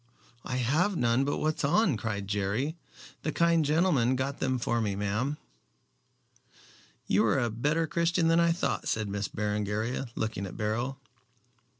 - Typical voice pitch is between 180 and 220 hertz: No, low, 125 Hz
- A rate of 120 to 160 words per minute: Yes, average, 155 wpm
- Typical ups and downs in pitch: No, wide, 6.6 semitones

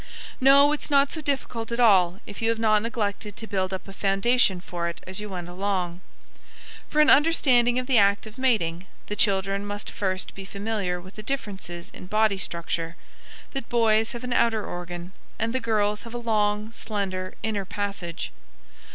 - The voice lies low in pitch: No, high, 210 Hz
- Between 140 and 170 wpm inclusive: No, average, 185 wpm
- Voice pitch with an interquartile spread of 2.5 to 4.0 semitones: Yes, average, 3.6 semitones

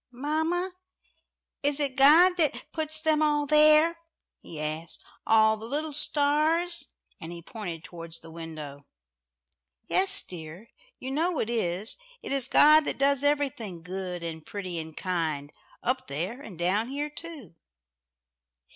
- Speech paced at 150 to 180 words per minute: No, average, 140 wpm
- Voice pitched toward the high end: Yes, very high, 250 Hz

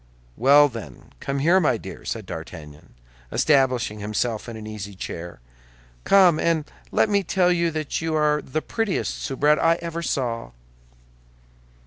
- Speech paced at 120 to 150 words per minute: Yes, average, 145 wpm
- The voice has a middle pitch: Yes, medium, 145 Hz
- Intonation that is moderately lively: No, wide, 6.5 semitones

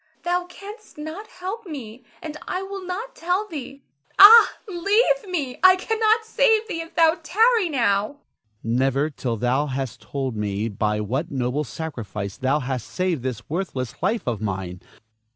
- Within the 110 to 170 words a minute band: Yes, average, 160 wpm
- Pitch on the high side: Yes, high, 245 Hz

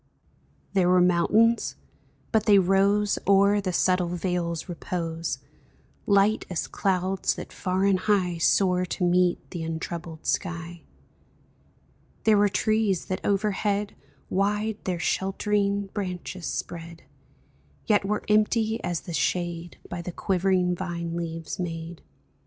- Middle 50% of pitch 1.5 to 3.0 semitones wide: Yes, average, 2.7 semitones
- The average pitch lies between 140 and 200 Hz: Yes, medium, 185 Hz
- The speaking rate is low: Yes, slow, 125 wpm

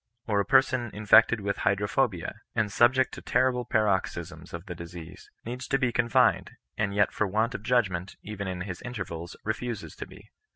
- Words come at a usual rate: Yes, average, 175 wpm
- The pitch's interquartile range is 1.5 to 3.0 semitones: No, average, 4.2 semitones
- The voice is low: Yes, low, 105 Hz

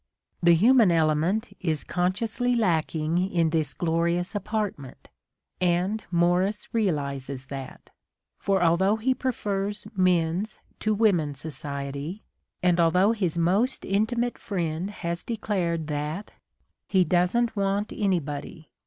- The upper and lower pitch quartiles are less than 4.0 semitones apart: No, average, 4.4 semitones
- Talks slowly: Yes, slow, 110 wpm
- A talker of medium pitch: Yes, medium, 180 Hz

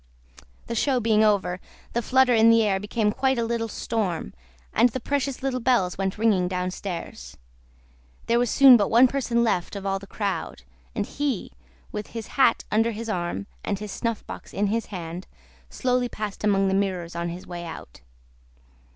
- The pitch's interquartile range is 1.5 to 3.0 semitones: No, average, 3.7 semitones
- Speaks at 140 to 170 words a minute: No, average, 180 wpm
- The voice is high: Yes, high, 215 Hz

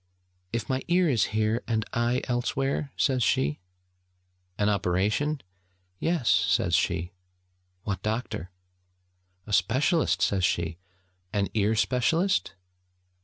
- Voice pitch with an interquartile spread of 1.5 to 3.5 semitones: No, average, 4.7 semitones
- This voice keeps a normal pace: No, slow, 110 wpm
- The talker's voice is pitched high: No, low, 110 Hz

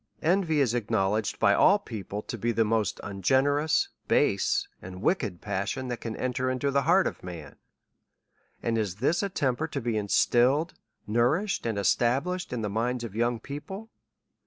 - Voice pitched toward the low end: Yes, low, 120 Hz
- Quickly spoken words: No, average, 170 wpm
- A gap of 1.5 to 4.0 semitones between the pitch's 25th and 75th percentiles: No, average, 5.2 semitones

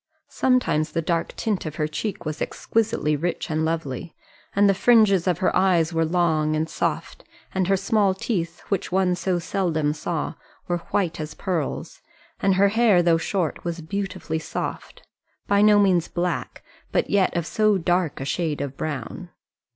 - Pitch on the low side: No, medium, 175 Hz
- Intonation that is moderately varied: Yes, average, 3.6 semitones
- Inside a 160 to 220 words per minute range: Yes, average, 170 wpm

